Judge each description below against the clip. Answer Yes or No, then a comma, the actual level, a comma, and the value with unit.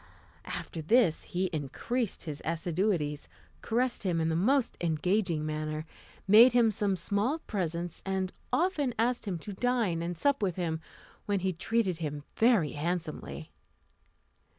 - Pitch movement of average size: No, wide, 5.9 semitones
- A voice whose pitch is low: No, medium, 185 Hz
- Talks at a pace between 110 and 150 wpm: Yes, average, 140 wpm